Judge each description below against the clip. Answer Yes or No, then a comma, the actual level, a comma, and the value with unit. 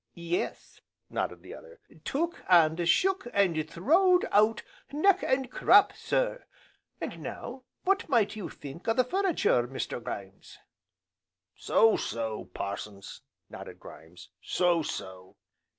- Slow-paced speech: Yes, slow, 120 wpm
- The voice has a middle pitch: No, high, 200 Hz